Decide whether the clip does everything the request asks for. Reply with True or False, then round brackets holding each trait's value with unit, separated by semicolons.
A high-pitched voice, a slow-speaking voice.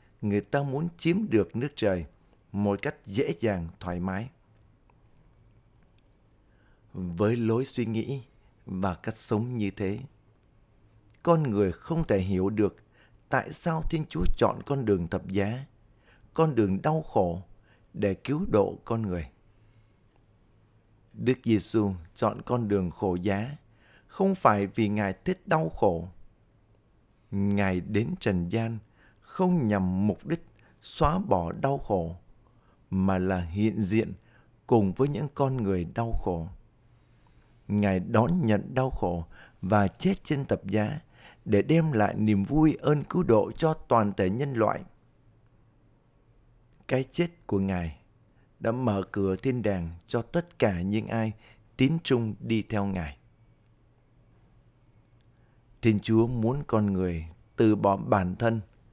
False (110 Hz; 135 wpm)